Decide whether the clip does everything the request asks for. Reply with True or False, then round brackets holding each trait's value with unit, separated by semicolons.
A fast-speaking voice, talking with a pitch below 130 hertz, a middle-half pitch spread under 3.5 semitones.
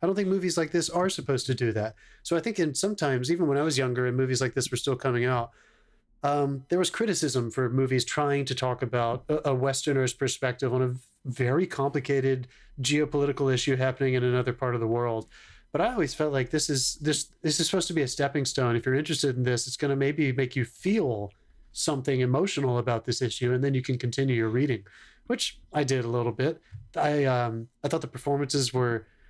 False (225 wpm; 135 Hz; 2.9 semitones)